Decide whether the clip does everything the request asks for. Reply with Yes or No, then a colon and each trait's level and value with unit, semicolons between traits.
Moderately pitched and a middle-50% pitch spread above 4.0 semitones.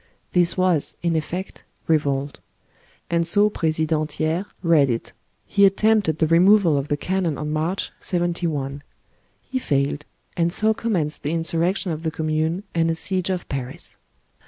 No: medium, 165 Hz; average, 3.2 semitones